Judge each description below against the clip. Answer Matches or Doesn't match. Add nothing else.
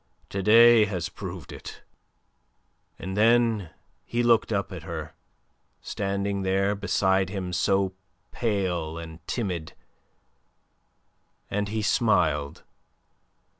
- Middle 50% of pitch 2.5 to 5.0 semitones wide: Matches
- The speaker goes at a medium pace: Doesn't match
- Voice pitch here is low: Matches